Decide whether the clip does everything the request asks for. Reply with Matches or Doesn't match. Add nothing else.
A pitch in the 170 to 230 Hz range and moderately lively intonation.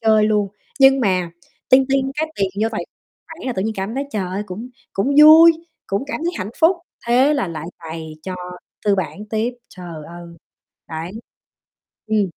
Doesn't match